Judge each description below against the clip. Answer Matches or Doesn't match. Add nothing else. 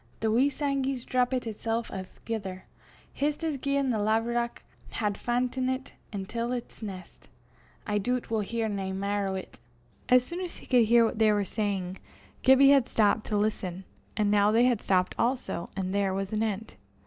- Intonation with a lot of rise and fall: Doesn't match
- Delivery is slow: Doesn't match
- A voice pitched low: Doesn't match